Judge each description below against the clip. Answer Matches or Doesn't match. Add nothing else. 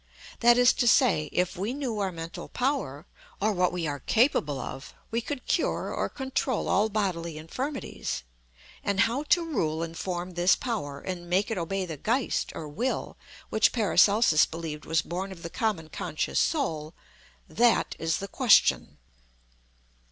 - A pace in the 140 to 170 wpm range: Matches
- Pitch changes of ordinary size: Doesn't match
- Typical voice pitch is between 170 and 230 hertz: Matches